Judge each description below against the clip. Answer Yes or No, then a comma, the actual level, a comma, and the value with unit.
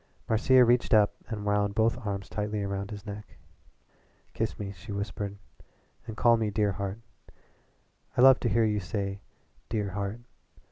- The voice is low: Yes, low, 105 Hz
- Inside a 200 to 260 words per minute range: No, average, 155 wpm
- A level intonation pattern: Yes, narrow, 2.0 semitones